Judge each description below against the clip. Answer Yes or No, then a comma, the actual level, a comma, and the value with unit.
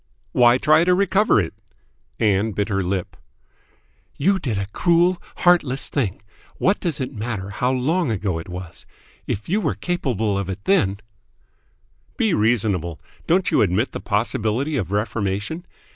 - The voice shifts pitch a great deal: Yes, wide, 8.6 semitones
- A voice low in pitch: Yes, low, 115 Hz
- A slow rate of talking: No, average, 155 wpm